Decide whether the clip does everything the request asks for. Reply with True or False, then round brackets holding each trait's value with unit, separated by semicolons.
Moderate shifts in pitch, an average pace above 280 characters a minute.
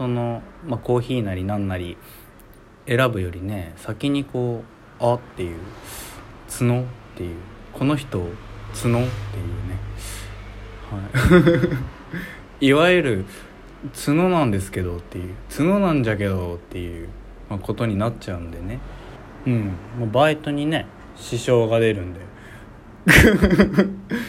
False (4.3 semitones; 250 characters per minute)